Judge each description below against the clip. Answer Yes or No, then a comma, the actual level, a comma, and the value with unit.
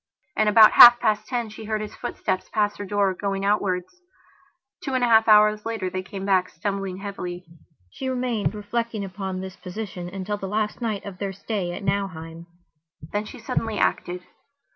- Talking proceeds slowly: No, average, 180 wpm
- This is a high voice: Yes, high, 205 Hz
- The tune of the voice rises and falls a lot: No, narrow, 2.5 semitones